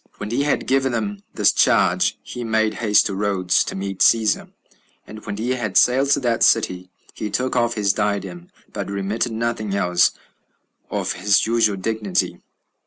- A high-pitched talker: No, low, 105 Hz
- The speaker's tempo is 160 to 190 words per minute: Yes, average, 175 wpm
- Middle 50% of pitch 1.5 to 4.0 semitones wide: Yes, average, 3.0 semitones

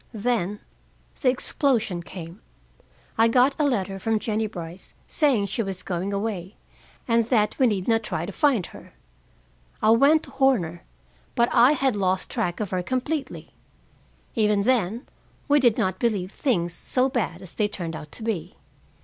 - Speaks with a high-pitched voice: Yes, high, 215 Hz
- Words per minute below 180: Yes, average, 165 wpm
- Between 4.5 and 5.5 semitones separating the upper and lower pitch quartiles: Yes, average, 5.1 semitones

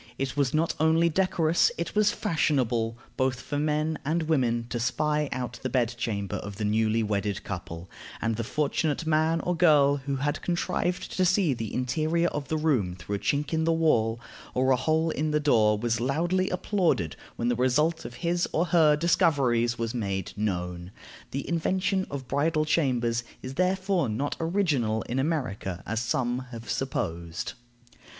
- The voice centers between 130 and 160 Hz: Yes, medium, 140 Hz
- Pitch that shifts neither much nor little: No, wide, 5.7 semitones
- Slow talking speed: No, average, 170 wpm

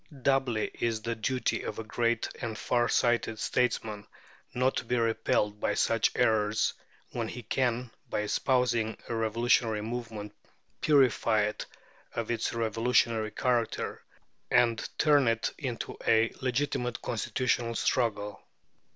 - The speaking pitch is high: No, low, 115 Hz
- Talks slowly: Yes, slow, 130 wpm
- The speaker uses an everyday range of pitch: No, narrow, 1.8 semitones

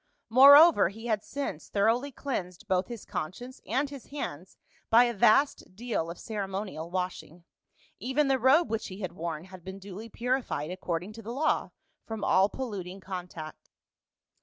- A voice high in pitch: Yes, high, 205 Hz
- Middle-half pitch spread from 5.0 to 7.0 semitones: Yes, average, 5.3 semitones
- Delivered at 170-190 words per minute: No, average, 160 wpm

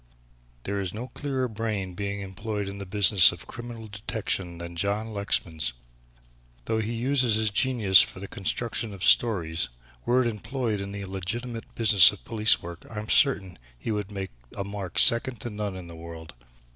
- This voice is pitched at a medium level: No, low, 105 Hz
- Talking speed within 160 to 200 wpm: Yes, average, 180 wpm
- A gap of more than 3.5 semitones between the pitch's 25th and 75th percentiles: No, average, 3.2 semitones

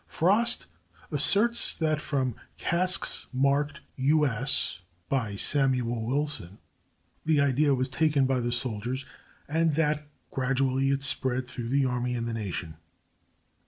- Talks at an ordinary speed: No, slow, 125 wpm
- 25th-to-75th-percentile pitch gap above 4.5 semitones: No, average, 3.3 semitones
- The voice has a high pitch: No, low, 135 Hz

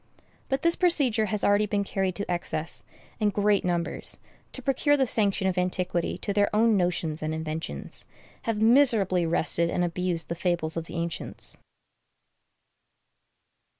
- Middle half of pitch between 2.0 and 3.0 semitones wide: No, average, 4.0 semitones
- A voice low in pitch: No, high, 190 Hz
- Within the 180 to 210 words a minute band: No, average, 150 wpm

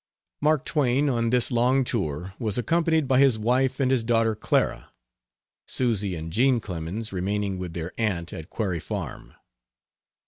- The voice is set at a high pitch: No, low, 115 Hz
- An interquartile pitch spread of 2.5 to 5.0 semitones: No, wide, 5.5 semitones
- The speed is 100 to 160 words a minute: Yes, average, 150 wpm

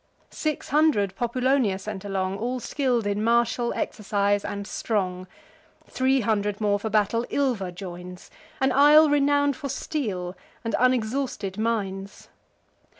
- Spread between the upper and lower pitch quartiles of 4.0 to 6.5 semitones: Yes, average, 4.8 semitones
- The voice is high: Yes, high, 220 Hz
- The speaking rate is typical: No, slow, 125 wpm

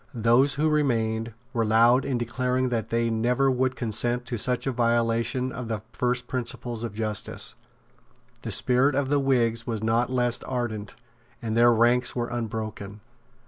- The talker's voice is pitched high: No, low, 120 Hz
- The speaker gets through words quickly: No, average, 160 wpm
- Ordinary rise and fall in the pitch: No, narrow, 1.9 semitones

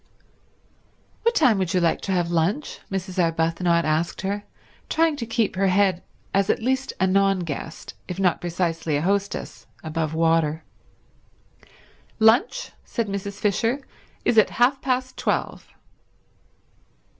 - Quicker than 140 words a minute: No, slow, 135 wpm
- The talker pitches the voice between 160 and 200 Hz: Yes, high, 190 Hz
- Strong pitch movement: No, average, 4.9 semitones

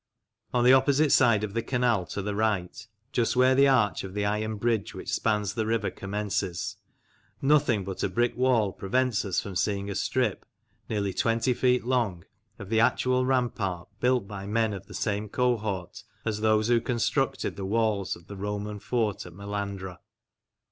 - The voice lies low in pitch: Yes, low, 110 Hz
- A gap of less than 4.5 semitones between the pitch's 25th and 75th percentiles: Yes, average, 3.3 semitones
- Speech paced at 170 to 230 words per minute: Yes, average, 175 wpm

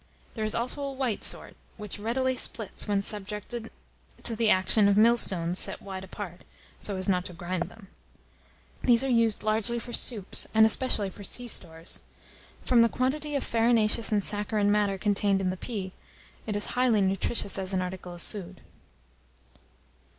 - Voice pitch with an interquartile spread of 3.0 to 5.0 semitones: Yes, average, 3.3 semitones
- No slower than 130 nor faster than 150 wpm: No, average, 170 wpm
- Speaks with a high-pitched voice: Yes, high, 210 Hz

